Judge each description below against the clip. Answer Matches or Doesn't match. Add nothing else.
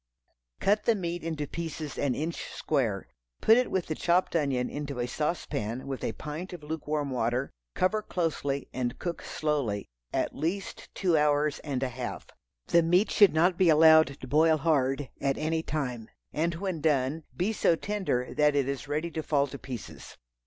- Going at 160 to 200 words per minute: Matches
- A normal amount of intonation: Matches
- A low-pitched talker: Doesn't match